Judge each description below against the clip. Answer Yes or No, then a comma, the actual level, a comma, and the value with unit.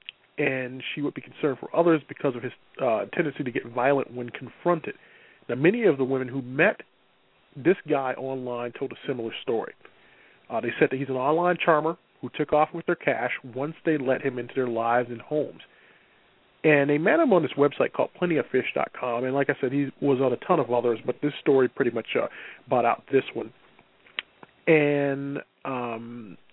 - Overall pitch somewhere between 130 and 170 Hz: Yes, low, 135 Hz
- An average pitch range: Yes, average, 3.2 semitones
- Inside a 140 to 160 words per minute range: No, average, 195 wpm